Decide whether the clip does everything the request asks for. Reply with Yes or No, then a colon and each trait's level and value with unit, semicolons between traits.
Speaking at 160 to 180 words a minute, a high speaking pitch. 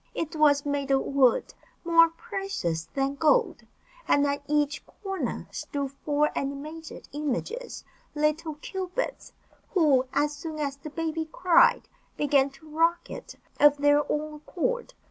No: slow, 135 wpm; very high, 300 Hz